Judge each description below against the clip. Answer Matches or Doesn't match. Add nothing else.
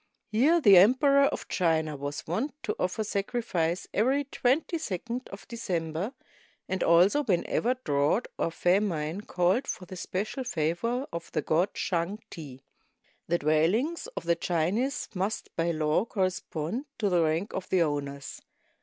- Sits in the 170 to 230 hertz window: Matches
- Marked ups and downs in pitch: Matches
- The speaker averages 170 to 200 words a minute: Doesn't match